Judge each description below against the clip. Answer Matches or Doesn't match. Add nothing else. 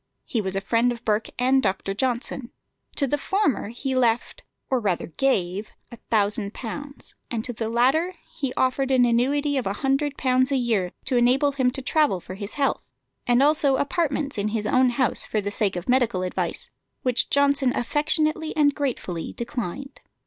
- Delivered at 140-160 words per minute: Doesn't match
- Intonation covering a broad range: Doesn't match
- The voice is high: Matches